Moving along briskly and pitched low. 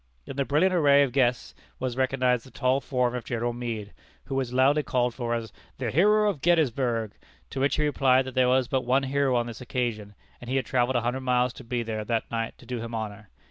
Yes: fast, 235 wpm; low, 125 Hz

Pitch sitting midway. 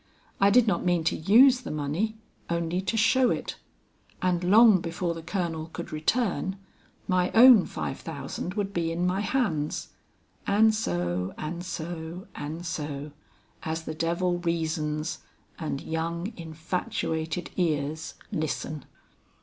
Yes: medium, 170 Hz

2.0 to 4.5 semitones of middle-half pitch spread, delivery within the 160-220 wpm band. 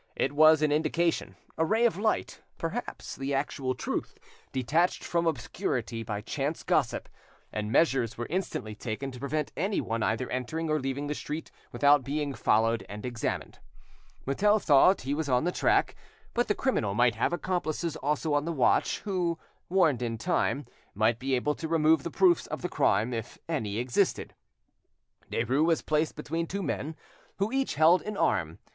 No: average, 5.2 semitones; average, 170 wpm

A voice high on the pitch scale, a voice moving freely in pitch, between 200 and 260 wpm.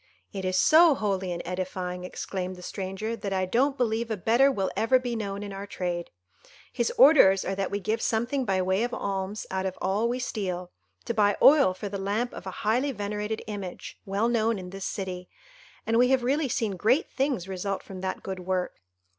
No: high, 200 Hz; average, 3.8 semitones; fast, 205 wpm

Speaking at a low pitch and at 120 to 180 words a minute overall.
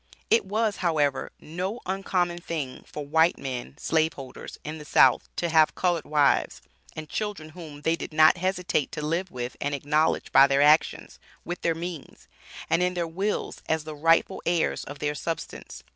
No: medium, 160 Hz; average, 175 wpm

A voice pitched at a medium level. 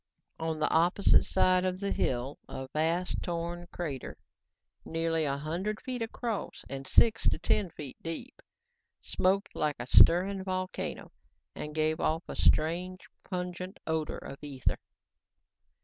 Yes: medium, 170 Hz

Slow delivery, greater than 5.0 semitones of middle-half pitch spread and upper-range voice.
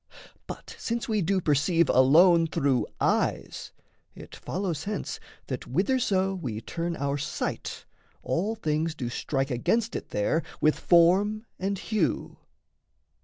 No: slow, 125 wpm; wide, 5.5 semitones; medium, 170 Hz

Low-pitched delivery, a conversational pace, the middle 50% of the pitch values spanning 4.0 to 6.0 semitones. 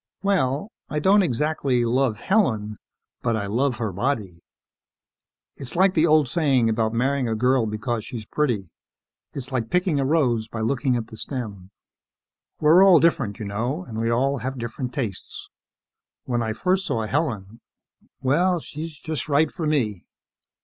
Yes: low, 130 Hz; average, 160 wpm; average, 5.2 semitones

